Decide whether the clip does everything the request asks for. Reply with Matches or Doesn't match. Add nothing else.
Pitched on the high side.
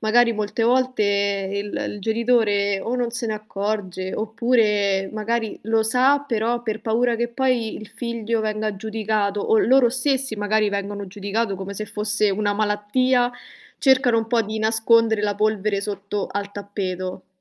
Matches